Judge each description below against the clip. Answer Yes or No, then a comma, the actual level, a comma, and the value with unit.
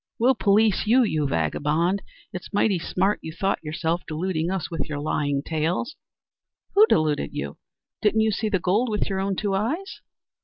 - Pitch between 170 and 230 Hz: Yes, high, 190 Hz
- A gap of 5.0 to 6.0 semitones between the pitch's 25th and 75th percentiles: Yes, average, 5.3 semitones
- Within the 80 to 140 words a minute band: No, average, 170 wpm